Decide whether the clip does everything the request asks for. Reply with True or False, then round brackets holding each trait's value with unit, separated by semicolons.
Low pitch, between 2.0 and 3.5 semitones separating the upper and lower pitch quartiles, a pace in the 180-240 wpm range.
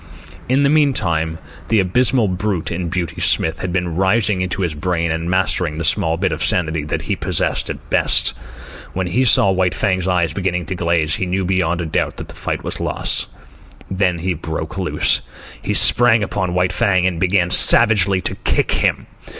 True (90 Hz; 2.4 semitones; 185 wpm)